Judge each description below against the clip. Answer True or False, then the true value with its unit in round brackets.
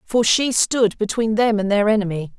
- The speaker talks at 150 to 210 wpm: True (200 wpm)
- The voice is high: True (215 Hz)